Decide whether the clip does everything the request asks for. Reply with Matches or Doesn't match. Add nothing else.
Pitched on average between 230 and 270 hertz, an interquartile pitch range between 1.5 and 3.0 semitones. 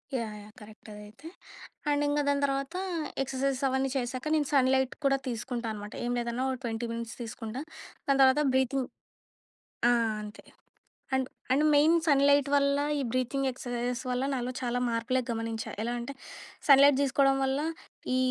Matches